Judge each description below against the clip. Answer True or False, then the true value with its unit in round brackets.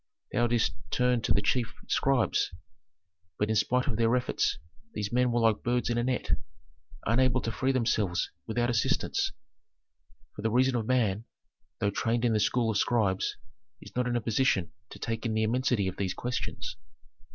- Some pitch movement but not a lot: False (2.3 semitones)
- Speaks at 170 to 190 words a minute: True (180 wpm)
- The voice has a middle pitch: False (115 Hz)